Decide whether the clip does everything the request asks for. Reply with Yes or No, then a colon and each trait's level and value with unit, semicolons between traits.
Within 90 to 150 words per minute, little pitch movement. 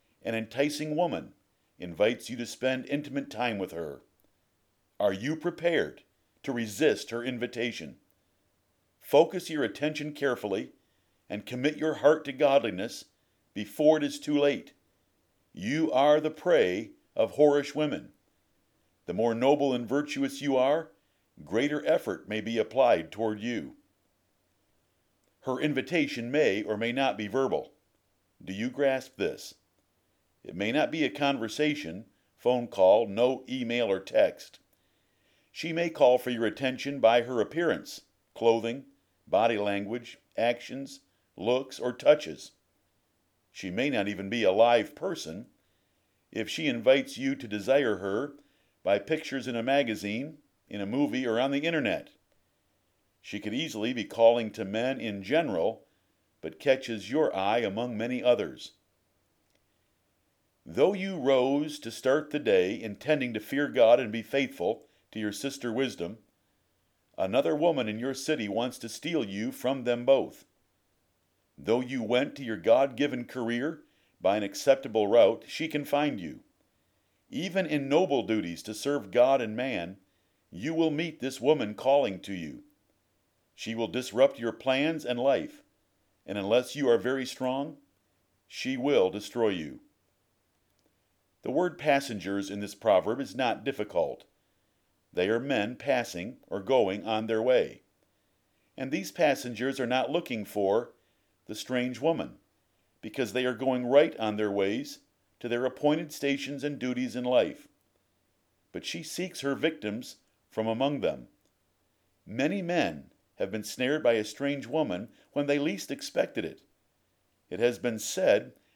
No: average, 145 wpm; average, 5.1 semitones